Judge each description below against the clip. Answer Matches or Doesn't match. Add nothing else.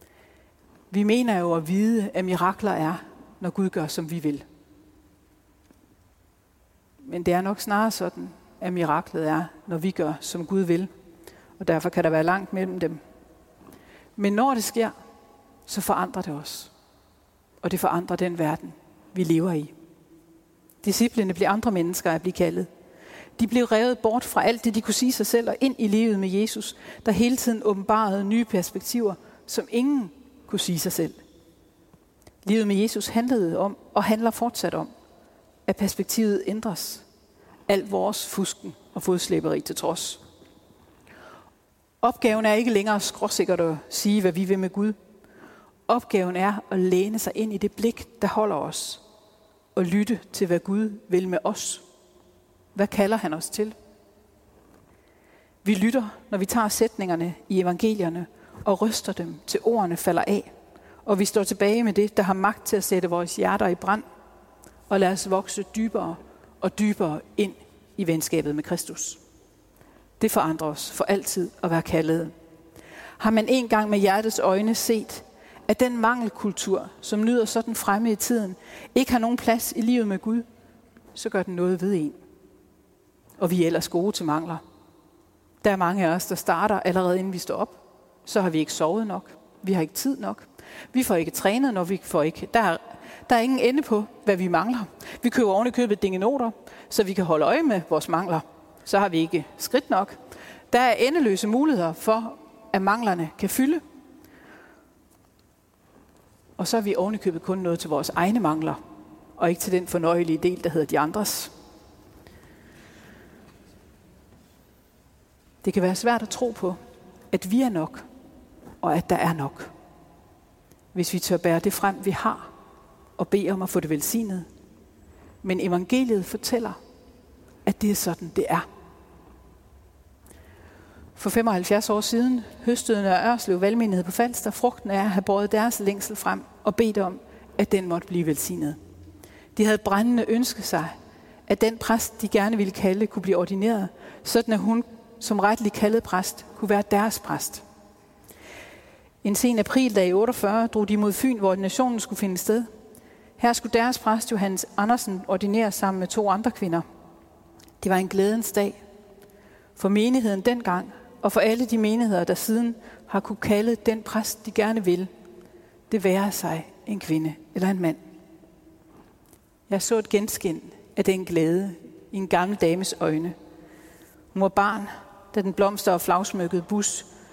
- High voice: Matches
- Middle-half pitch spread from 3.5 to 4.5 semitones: Matches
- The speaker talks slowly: Doesn't match